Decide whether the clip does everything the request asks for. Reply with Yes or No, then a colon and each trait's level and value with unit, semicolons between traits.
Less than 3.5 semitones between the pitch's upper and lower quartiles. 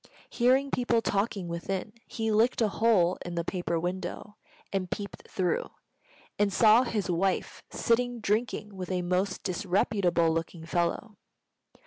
No: average, 4.0 semitones